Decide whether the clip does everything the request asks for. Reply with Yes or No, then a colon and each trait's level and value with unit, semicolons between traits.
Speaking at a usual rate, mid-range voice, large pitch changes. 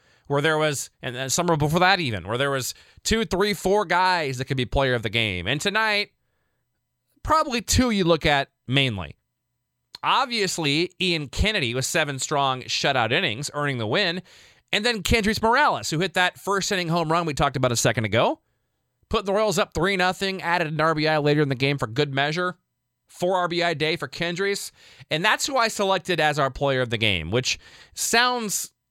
Yes: average, 195 wpm; medium, 160 Hz; wide, 6.0 semitones